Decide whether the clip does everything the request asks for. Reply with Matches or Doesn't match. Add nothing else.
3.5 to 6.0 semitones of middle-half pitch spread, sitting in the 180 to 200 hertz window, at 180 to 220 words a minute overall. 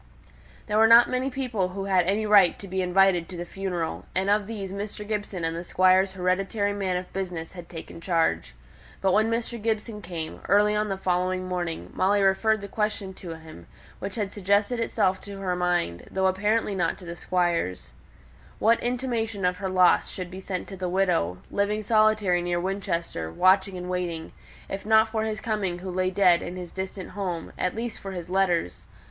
Doesn't match